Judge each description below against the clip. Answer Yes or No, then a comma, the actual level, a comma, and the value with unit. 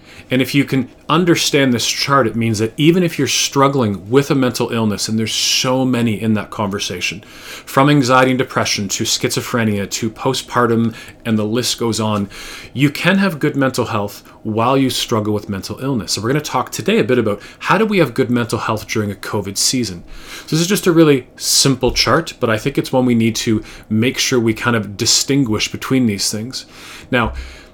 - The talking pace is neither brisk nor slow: No, fast, 210 wpm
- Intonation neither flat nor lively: Yes, average, 3.9 semitones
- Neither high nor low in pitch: No, low, 120 Hz